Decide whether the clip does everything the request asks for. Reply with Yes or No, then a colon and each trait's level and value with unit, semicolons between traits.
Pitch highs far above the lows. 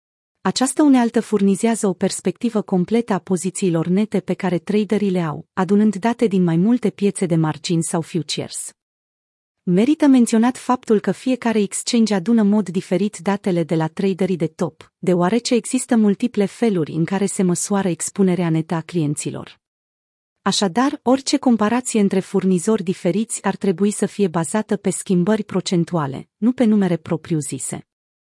No: average, 3.6 semitones